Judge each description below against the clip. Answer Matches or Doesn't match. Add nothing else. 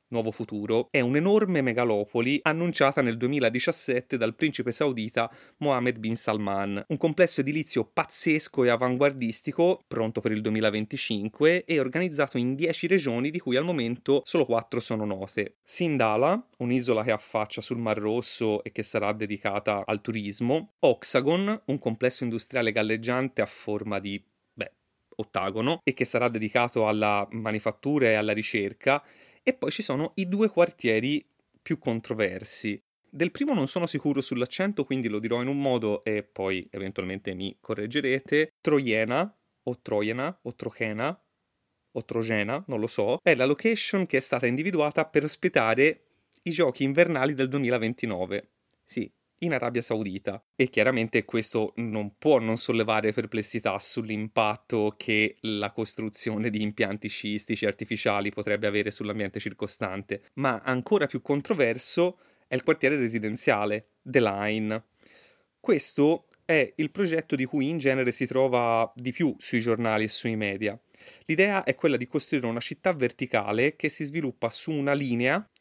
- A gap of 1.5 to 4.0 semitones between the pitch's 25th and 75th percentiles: Doesn't match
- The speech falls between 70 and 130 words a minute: Doesn't match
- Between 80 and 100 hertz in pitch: Doesn't match